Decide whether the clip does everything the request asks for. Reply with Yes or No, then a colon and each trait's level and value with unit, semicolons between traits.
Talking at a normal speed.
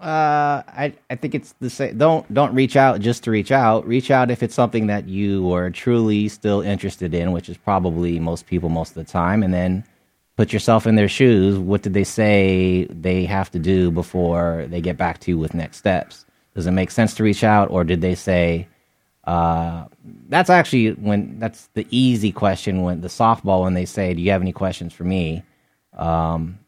No: fast, 210 wpm